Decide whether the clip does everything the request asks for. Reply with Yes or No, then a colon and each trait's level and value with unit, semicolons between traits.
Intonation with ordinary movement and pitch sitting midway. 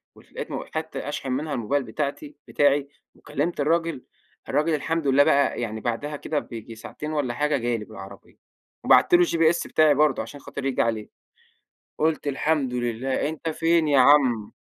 Yes: average, 4.0 semitones; medium, 145 Hz